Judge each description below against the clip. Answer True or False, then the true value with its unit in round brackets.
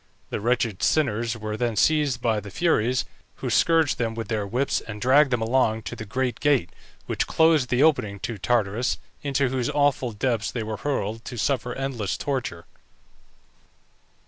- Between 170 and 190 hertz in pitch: False (120 Hz)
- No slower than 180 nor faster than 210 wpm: False (170 wpm)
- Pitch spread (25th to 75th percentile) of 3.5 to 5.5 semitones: True (3.8 semitones)